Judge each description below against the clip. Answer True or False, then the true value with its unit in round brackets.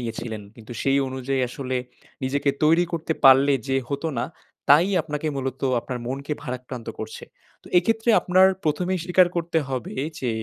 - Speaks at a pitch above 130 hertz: True (140 Hz)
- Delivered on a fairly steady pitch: False (4.4 semitones)